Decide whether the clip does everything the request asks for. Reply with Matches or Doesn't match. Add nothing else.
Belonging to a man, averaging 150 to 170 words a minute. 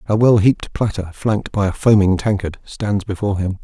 Doesn't match